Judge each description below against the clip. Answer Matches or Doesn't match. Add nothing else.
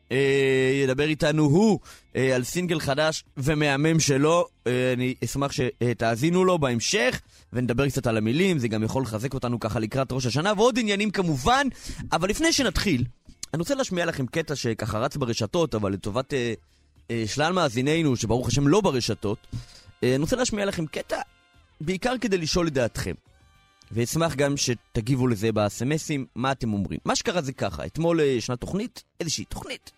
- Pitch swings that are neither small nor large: Doesn't match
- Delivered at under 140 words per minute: Doesn't match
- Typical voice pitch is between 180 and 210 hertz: Doesn't match